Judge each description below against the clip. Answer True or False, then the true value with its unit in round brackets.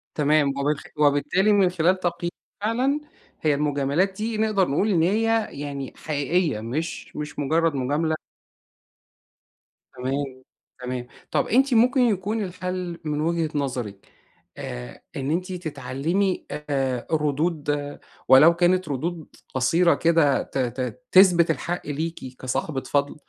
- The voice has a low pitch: False (160 Hz)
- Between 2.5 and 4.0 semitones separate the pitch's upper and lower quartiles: False (4.6 semitones)